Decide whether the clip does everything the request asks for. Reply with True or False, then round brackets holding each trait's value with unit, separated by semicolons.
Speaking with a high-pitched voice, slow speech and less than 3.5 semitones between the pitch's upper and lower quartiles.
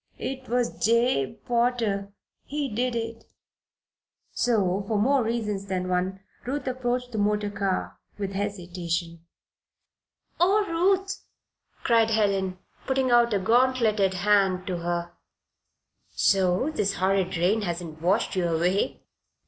False (205 Hz; 125 wpm; 4.6 semitones)